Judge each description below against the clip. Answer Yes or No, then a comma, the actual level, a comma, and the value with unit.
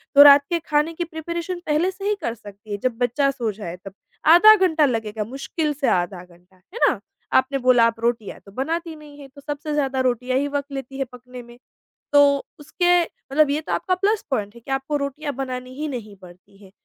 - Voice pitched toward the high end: Yes, very high, 275 Hz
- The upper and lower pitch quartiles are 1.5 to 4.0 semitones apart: No, average, 4.5 semitones